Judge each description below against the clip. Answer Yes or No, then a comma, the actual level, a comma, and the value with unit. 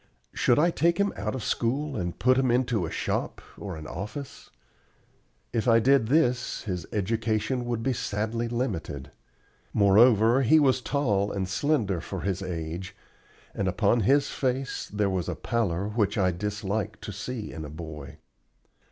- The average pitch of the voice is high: No, low, 110 Hz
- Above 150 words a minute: Yes, average, 160 wpm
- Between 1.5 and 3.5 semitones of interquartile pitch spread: No, average, 5.1 semitones